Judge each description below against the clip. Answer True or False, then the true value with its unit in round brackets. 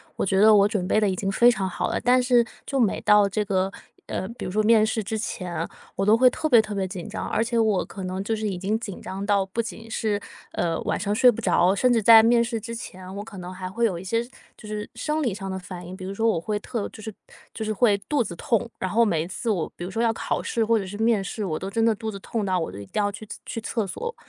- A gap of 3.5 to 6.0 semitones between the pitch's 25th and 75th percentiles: False (3.1 semitones)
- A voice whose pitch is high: True (210 Hz)